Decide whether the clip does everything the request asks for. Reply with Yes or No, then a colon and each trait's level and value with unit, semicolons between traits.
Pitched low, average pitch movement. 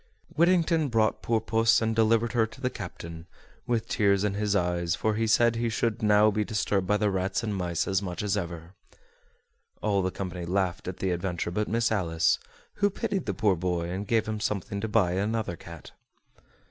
Yes: low, 105 Hz; average, 3.8 semitones